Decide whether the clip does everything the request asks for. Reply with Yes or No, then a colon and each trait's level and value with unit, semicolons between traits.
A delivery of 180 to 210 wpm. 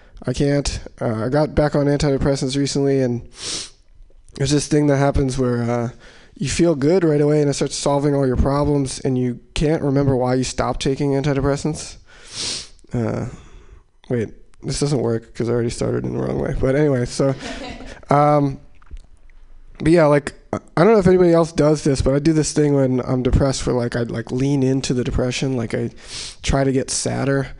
Yes: average, 190 wpm